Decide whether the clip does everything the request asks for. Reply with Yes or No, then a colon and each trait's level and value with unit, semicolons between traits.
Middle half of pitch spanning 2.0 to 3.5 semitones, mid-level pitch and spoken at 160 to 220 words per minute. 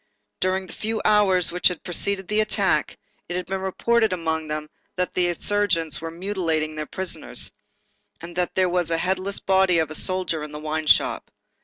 Yes: average, 2.8 semitones; medium, 180 Hz; average, 185 wpm